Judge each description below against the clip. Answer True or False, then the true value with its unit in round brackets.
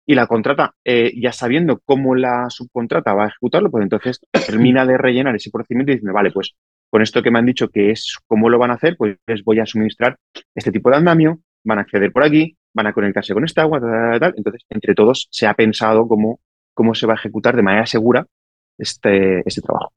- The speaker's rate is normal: False (230 wpm)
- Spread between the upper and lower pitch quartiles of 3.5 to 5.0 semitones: False (3.1 semitones)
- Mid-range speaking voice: False (115 Hz)